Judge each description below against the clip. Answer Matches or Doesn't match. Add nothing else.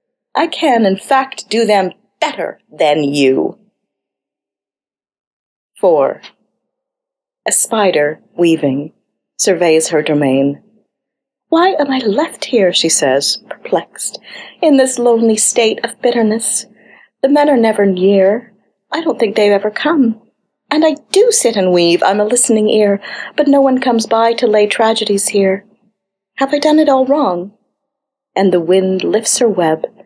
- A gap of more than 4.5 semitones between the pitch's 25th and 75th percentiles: Matches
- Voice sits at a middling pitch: Doesn't match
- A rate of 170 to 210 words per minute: Doesn't match